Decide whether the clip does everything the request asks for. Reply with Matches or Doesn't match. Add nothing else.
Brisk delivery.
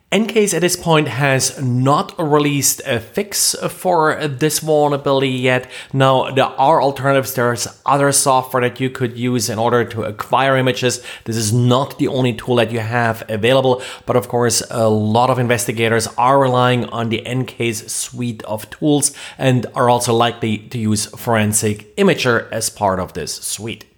Doesn't match